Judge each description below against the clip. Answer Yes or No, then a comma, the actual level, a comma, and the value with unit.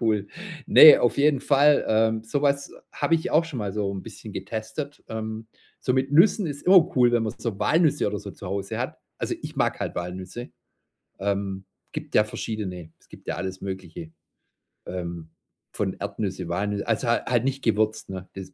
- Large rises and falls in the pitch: Yes, wide, 5.7 semitones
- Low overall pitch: Yes, low, 110 Hz